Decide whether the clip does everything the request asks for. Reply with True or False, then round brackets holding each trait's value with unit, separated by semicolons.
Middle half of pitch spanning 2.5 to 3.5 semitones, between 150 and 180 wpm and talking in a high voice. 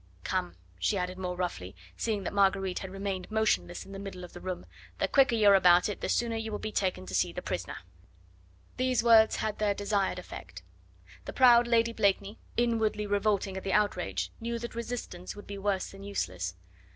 False (2.9 semitones; 200 wpm; 200 Hz)